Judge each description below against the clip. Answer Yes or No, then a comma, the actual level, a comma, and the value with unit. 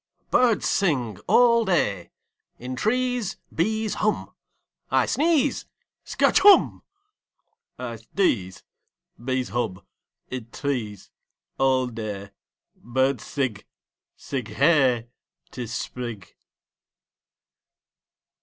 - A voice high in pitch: No, low, 130 Hz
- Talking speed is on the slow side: Yes, slow, 85 wpm